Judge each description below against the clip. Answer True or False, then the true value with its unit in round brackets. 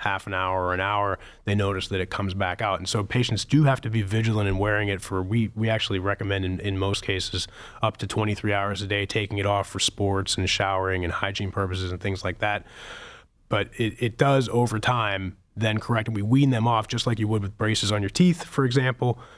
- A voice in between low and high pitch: False (100 Hz)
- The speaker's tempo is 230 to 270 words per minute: True (240 wpm)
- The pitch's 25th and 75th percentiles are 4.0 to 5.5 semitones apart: False (2.6 semitones)